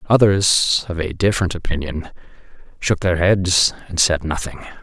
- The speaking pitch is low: Yes, very low, 90 Hz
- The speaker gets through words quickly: No, slow, 135 wpm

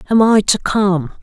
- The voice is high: Yes, high, 200 Hz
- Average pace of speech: Yes, average, 195 wpm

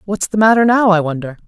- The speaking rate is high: Yes, fast, 245 wpm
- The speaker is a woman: Yes, female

